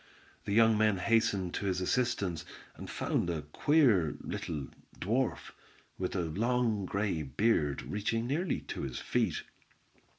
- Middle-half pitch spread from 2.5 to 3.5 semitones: No, average, 4.9 semitones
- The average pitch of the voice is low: Yes, low, 100 Hz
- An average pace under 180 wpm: Yes, slow, 135 wpm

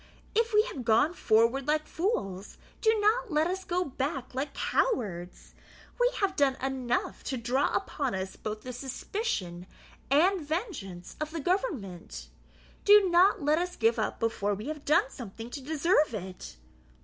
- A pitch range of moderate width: No, wide, 8.1 semitones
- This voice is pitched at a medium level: No, very high, 275 Hz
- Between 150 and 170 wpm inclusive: Yes, average, 160 wpm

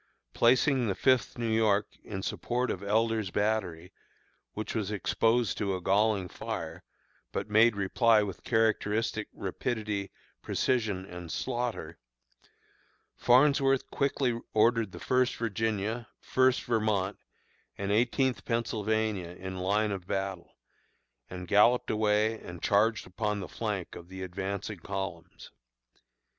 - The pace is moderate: No, slow, 120 wpm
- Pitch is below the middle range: Yes, low, 105 Hz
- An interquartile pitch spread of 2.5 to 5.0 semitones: Yes, average, 3.1 semitones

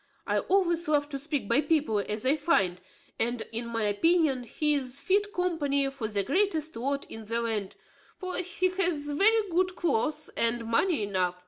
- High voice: Yes, very high, 285 Hz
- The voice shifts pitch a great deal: Yes, wide, 6.9 semitones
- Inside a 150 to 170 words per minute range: No, average, 180 wpm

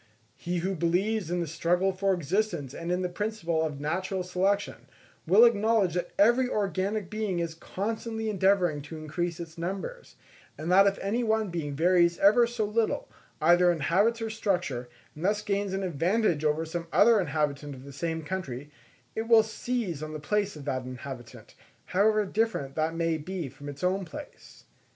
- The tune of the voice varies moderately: Yes, average, 4.6 semitones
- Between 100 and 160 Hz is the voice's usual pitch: No, medium, 180 Hz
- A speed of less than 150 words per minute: No, average, 180 wpm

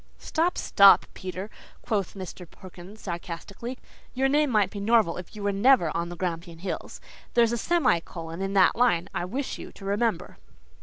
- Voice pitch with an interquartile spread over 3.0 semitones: Yes, average, 5.1 semitones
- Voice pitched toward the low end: No, high, 195 Hz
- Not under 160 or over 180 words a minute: Yes, average, 175 wpm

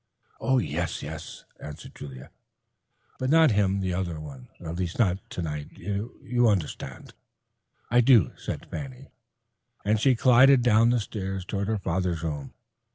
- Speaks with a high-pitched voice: No, very low, 95 Hz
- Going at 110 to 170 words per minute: Yes, average, 140 wpm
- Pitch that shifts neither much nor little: No, wide, 6.4 semitones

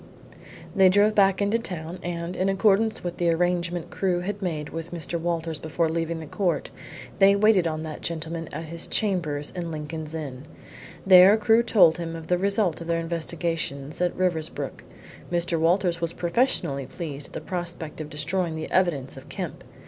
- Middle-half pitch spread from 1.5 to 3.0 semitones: Yes, narrow, 2.6 semitones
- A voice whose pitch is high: No, medium, 170 Hz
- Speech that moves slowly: No, average, 175 wpm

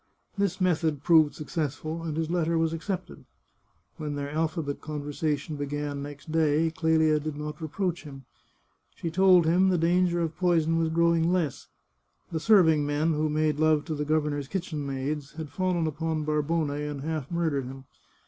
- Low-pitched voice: No, medium, 155 Hz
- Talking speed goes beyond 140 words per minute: Yes, average, 165 wpm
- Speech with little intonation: Yes, narrow, 2.1 semitones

